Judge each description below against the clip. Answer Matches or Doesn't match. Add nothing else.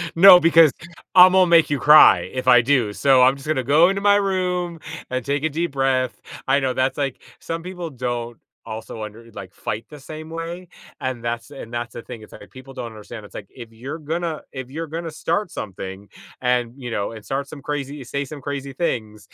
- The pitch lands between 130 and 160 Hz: Matches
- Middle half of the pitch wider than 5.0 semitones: Matches